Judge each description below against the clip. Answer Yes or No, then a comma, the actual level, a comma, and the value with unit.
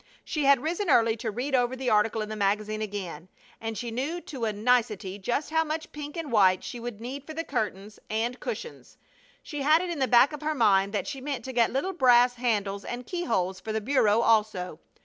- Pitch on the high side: Yes, high, 240 Hz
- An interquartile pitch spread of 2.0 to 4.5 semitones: No, average, 4.9 semitones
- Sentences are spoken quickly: Yes, fast, 225 wpm